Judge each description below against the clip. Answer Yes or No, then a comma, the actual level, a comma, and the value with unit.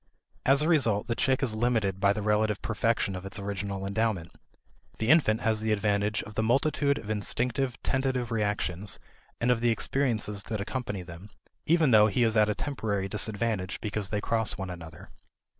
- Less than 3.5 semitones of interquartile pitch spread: Yes, average, 2.9 semitones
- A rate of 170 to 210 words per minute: Yes, average, 180 wpm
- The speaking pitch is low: Yes, low, 110 Hz